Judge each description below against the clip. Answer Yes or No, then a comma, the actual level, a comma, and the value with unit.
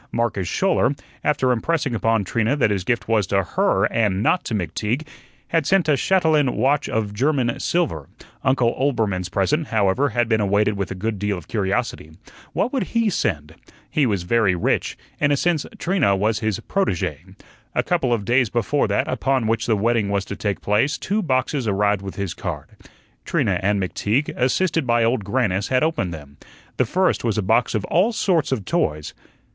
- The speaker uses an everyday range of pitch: No, wide, 6.1 semitones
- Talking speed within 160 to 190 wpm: Yes, average, 185 wpm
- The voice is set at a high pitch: No, low, 115 Hz